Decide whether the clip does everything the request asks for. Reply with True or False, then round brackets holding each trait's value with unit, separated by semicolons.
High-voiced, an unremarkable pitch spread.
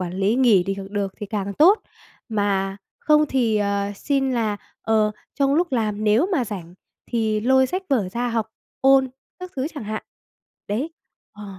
True (220 Hz; 4.6 semitones)